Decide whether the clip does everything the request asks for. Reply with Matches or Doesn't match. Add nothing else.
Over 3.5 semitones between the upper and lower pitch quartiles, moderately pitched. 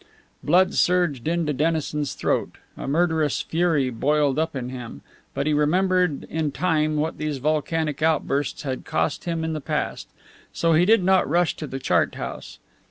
Doesn't match